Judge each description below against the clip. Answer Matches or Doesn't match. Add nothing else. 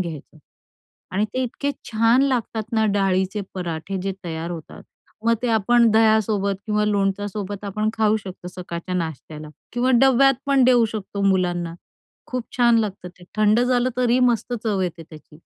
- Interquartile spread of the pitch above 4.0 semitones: Matches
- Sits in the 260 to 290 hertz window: Doesn't match